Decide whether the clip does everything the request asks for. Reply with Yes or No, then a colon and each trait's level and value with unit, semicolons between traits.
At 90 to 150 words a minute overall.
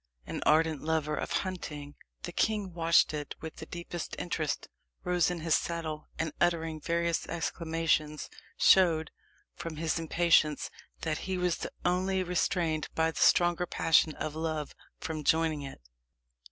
Yes: average, 140 wpm